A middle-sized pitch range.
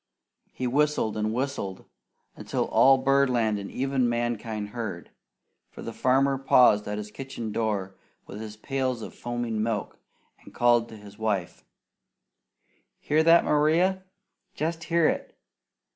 Yes: average, 4.2 semitones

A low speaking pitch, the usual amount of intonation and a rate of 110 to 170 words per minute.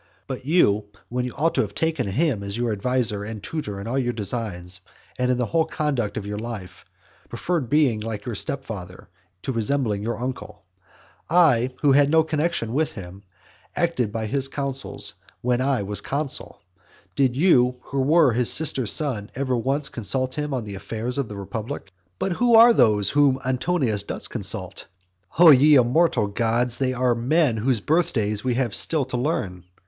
No: low, 125 Hz; average, 4.8 semitones; average, 180 wpm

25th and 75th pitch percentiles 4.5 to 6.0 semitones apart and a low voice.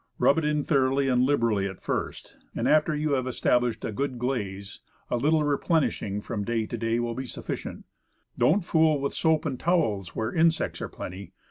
Yes: average, 5.0 semitones; low, 130 Hz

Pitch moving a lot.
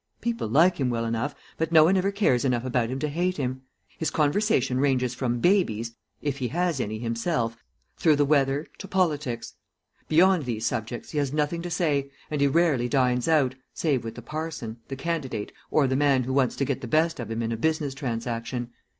No: average, 4.7 semitones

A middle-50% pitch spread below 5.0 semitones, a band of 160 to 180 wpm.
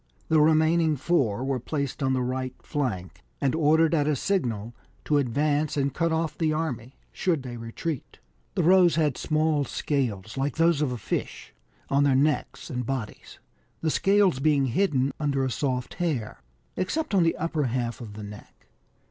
Yes: average, 4.1 semitones; average, 175 wpm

